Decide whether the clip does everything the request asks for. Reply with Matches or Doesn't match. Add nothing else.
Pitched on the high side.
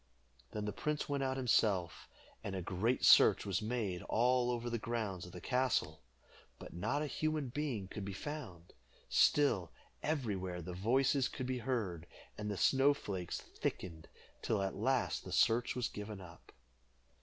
Doesn't match